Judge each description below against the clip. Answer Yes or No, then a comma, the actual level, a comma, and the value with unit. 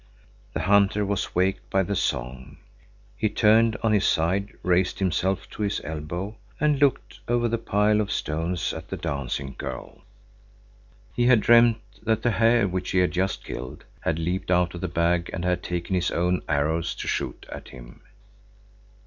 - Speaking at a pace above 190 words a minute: No, average, 175 wpm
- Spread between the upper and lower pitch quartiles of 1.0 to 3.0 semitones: No, average, 4.1 semitones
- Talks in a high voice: No, very low, 95 Hz